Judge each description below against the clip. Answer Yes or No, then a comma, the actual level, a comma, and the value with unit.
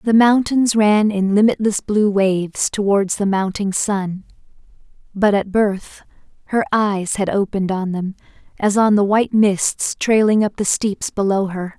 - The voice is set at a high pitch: Yes, high, 205 Hz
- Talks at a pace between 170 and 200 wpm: No, average, 155 wpm